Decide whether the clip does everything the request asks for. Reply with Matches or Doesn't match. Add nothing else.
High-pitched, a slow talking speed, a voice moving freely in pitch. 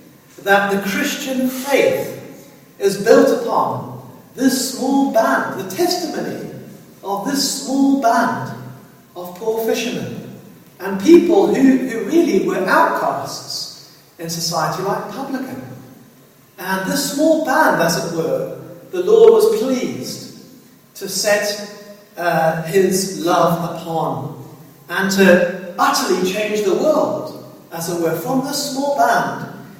Matches